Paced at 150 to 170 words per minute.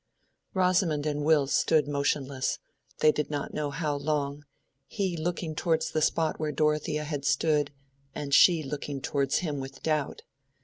No: average, 140 wpm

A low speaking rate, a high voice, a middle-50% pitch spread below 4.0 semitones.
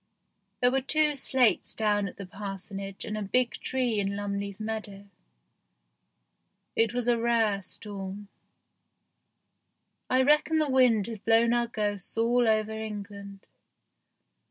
Yes: slow, 130 wpm; high, 220 Hz; average, 3.1 semitones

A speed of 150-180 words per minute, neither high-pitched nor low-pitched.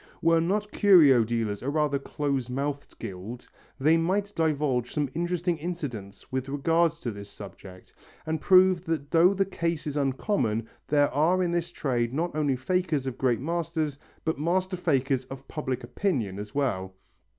Yes: average, 160 wpm; medium, 145 Hz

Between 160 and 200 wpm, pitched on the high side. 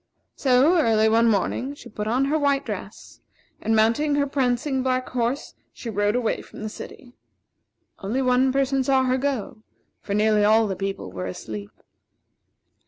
Yes: average, 165 wpm; high, 245 Hz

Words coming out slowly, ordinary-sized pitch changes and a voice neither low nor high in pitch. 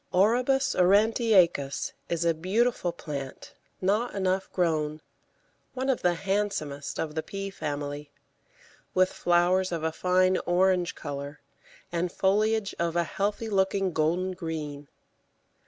Yes: slow, 120 wpm; average, 3.6 semitones; medium, 180 Hz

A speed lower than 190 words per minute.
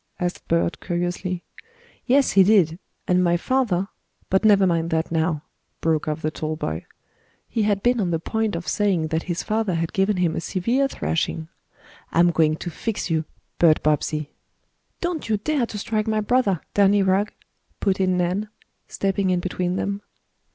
Yes: average, 170 wpm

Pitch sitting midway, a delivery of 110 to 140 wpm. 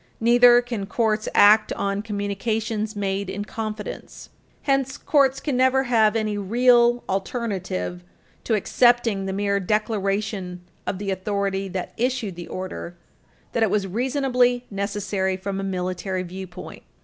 No: high, 205 Hz; slow, 135 wpm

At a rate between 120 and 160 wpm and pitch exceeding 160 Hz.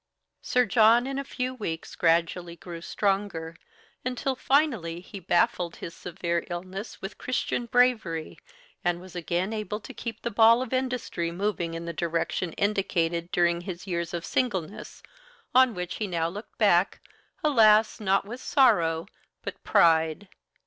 Yes: average, 150 wpm; high, 190 Hz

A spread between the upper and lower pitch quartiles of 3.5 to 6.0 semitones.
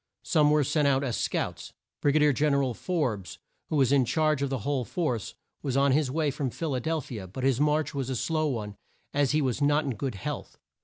No: average, 2.8 semitones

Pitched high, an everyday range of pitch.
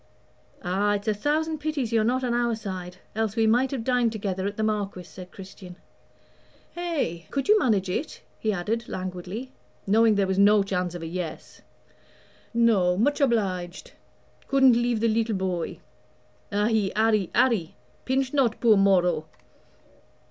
Yes: high, 215 Hz; average, 4.2 semitones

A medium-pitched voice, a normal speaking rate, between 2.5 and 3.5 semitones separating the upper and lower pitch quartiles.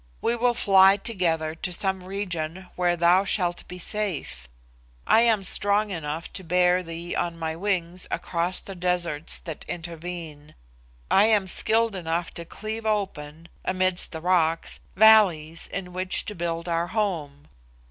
Yes: medium, 180 Hz; average, 145 wpm; average, 2.9 semitones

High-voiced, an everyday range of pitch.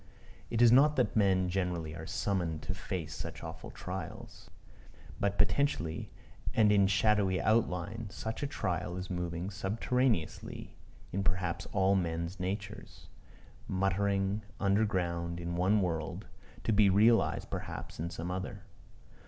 No: very low, 95 Hz; average, 3.0 semitones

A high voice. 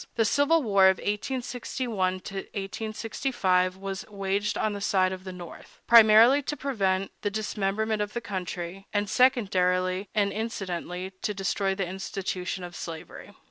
Yes: high, 195 Hz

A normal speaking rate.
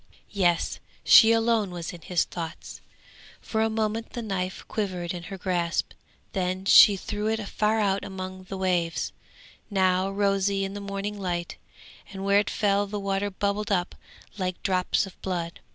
Yes: average, 165 wpm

